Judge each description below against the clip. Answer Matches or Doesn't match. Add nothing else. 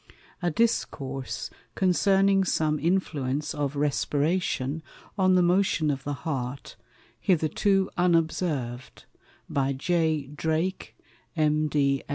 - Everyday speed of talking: Doesn't match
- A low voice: Doesn't match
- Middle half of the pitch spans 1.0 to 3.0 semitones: Doesn't match